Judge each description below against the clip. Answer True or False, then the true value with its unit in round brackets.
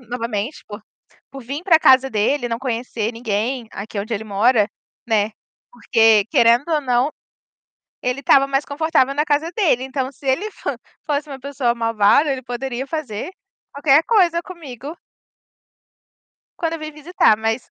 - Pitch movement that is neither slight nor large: True (4.2 semitones)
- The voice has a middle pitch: False (260 Hz)